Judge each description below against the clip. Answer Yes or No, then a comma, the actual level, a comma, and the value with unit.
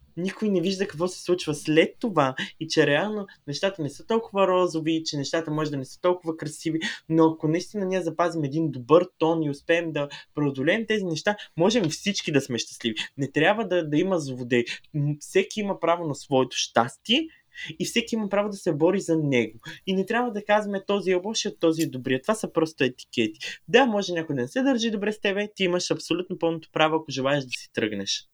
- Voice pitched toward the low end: No, medium, 165 Hz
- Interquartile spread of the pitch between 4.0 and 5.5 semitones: Yes, average, 4.8 semitones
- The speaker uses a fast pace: Yes, fast, 210 wpm